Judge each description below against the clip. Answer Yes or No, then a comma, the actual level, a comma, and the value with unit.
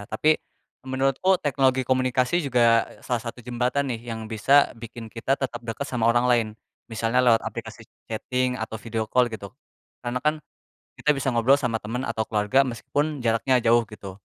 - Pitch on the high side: No, low, 120 Hz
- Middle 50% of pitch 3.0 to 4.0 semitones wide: No, narrow, 2.6 semitones